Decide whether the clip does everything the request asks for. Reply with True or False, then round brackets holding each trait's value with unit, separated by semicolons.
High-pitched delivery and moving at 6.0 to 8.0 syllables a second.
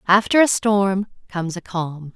False (195 Hz; 4.6 syllables/s)